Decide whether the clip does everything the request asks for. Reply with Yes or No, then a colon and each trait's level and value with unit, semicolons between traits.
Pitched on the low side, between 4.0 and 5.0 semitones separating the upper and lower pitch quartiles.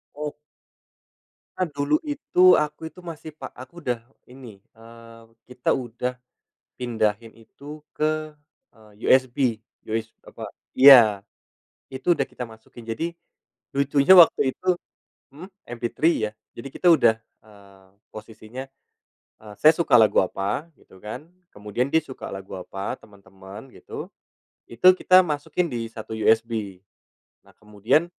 Yes: low, 115 Hz; average, 4.7 semitones